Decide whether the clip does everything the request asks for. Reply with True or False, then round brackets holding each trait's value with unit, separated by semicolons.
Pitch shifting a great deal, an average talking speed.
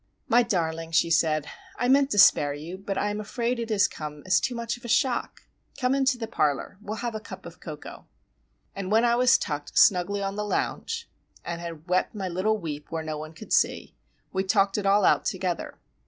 False (5.9 semitones; 215 wpm)